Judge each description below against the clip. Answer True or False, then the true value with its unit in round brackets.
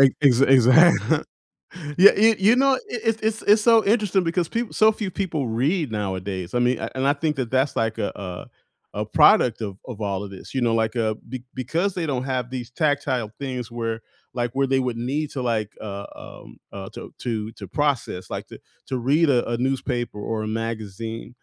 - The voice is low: True (125 Hz)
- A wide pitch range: True (5.7 semitones)